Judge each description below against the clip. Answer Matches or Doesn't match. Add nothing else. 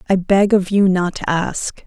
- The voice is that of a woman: Matches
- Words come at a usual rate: Doesn't match